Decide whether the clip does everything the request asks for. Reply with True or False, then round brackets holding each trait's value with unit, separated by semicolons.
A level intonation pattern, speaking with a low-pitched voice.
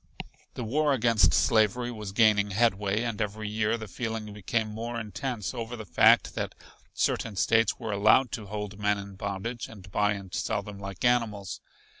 True (2.3 semitones; 110 Hz)